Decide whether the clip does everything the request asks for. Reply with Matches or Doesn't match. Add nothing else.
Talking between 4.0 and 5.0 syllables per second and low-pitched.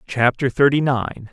Matches